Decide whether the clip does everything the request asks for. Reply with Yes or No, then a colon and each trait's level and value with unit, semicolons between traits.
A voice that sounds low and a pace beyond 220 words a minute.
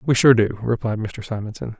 No: low, 115 Hz; average, 200 wpm